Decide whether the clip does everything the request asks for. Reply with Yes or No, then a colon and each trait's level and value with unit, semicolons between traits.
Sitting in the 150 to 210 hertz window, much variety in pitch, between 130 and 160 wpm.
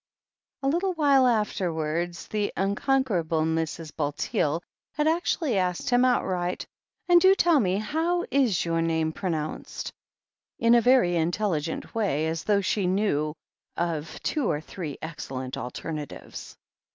Yes: medium, 185 Hz; wide, 7.5 semitones; slow, 135 wpm